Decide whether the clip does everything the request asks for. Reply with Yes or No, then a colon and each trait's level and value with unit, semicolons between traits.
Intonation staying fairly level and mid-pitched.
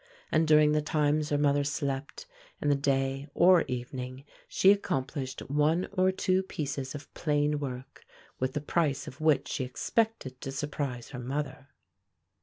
Yes: narrow, 2.3 semitones; medium, 145 Hz